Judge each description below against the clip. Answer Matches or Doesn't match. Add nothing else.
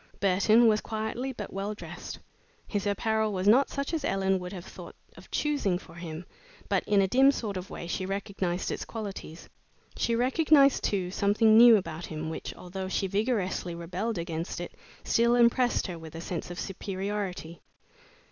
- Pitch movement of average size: Matches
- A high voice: Matches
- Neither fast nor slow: Matches